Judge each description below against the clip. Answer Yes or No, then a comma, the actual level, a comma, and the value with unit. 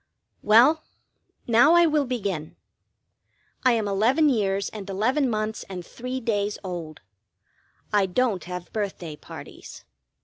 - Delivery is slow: Yes, slow, 125 wpm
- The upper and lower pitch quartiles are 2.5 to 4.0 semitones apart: No, average, 4.7 semitones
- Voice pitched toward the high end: Yes, high, 215 Hz